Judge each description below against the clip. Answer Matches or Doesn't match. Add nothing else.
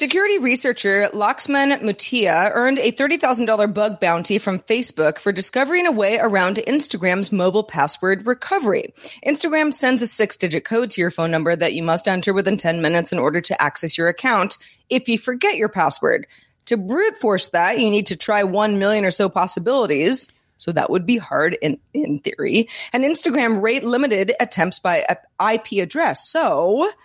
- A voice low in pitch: Doesn't match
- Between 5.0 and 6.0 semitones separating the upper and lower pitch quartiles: Matches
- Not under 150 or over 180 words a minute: Matches